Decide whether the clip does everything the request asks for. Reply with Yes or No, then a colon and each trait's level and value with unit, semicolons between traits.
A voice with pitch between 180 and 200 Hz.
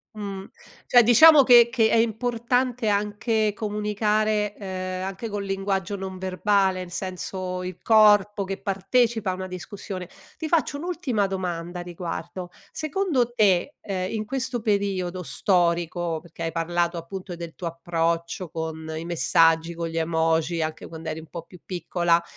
Yes: high, 190 Hz